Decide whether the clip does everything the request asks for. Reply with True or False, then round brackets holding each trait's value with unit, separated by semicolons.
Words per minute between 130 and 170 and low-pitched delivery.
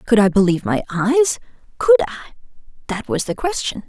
False (140 wpm; 225 Hz)